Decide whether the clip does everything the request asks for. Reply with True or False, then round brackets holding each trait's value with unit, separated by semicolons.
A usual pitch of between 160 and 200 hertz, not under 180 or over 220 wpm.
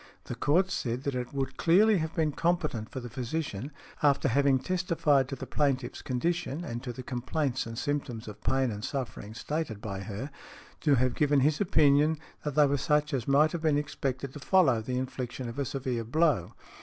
False (140 Hz; 195 wpm)